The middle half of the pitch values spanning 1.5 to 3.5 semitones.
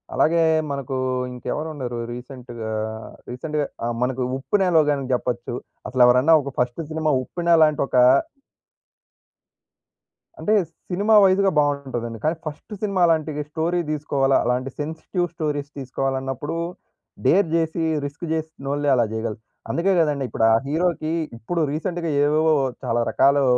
No: average, 4.1 semitones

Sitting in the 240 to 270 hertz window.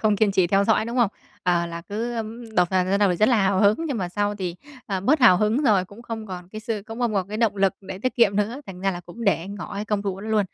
No: high, 205 Hz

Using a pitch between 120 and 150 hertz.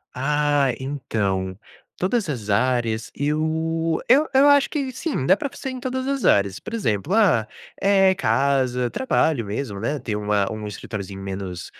Yes: medium, 140 Hz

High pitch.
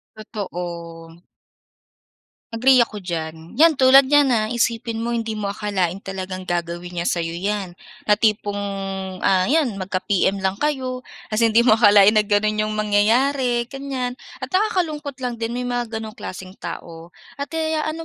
Yes: high, 215 Hz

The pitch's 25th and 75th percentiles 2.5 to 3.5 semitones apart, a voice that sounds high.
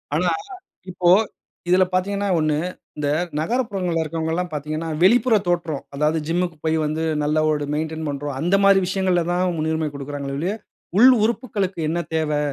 No: average, 3.2 semitones; medium, 165 Hz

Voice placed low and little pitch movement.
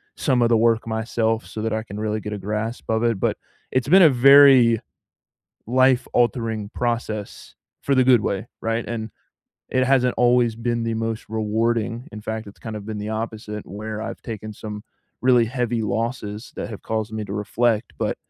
Yes: low, 115 Hz; narrow, 2.0 semitones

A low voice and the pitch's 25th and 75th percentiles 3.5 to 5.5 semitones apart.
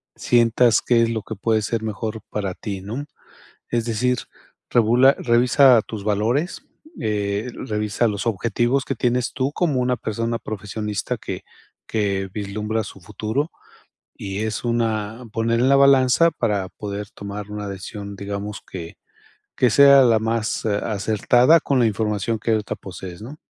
No: low, 110 Hz; average, 2.9 semitones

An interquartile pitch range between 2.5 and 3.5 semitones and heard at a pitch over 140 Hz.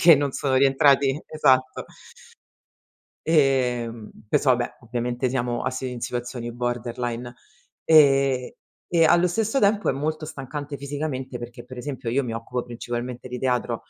No: average, 2.8 semitones; low, 130 Hz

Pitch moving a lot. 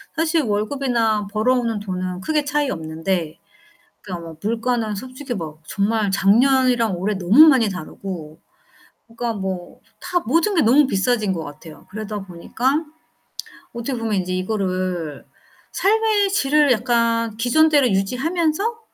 Yes: wide, 6.0 semitones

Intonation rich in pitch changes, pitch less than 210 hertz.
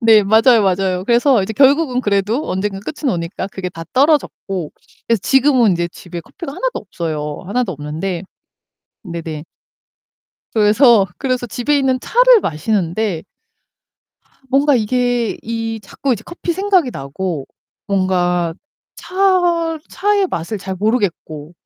No: wide, 6.8 semitones; high, 215 Hz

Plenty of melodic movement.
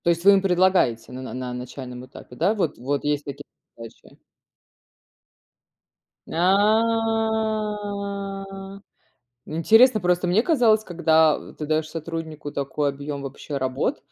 Yes: wide, 6.1 semitones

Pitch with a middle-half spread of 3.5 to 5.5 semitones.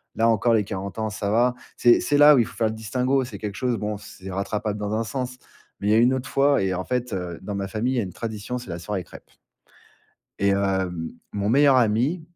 Yes: average, 4.0 semitones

